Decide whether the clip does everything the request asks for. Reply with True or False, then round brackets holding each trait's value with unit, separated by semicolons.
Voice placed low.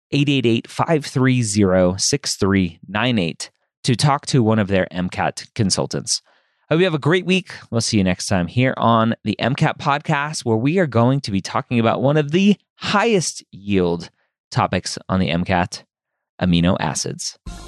True (115 Hz)